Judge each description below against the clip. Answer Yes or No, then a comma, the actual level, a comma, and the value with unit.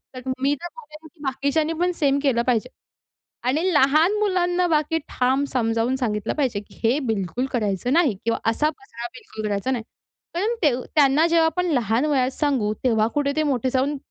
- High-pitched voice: Yes, very high, 270 Hz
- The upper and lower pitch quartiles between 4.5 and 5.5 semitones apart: Yes, average, 4.8 semitones